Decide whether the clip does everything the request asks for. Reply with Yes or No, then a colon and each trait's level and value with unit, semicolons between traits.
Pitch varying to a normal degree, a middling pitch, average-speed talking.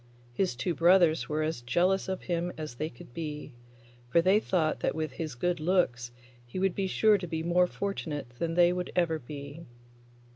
Yes: average, 3.0 semitones; medium, 165 Hz; average, 190 wpm